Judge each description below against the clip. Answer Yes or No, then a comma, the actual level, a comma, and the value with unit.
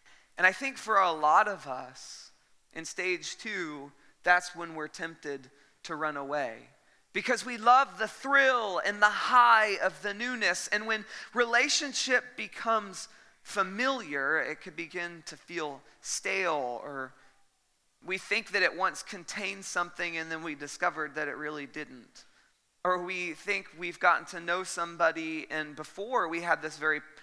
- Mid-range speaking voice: Yes, medium, 175 Hz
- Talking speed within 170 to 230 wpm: No, average, 155 wpm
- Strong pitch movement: Yes, wide, 5.7 semitones